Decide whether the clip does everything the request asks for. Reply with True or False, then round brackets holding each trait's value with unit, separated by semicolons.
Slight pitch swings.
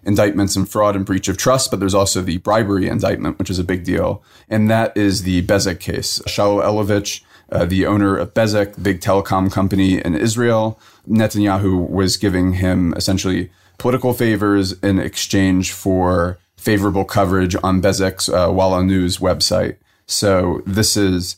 True (1.8 semitones)